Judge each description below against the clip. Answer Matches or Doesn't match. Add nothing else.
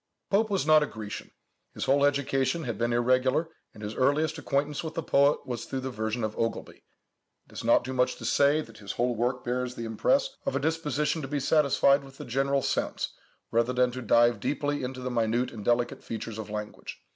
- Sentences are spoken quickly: Matches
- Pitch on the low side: Matches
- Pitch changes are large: Doesn't match